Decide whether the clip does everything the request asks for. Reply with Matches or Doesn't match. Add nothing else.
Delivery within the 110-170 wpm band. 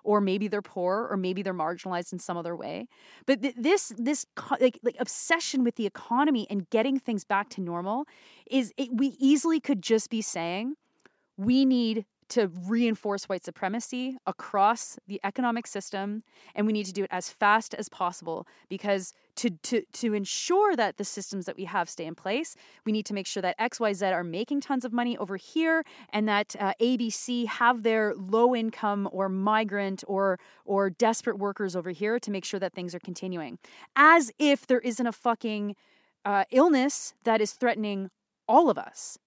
Doesn't match